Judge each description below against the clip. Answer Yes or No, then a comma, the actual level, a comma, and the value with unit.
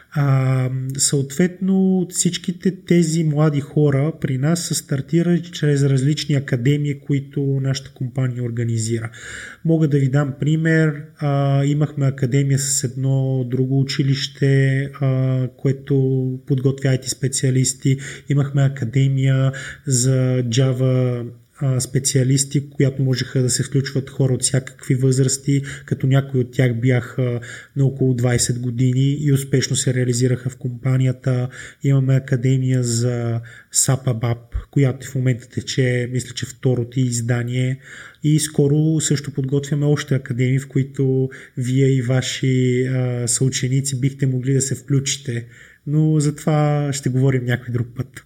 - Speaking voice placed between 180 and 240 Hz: No, low, 135 Hz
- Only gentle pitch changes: Yes, narrow, 1.7 semitones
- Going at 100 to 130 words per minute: Yes, average, 125 wpm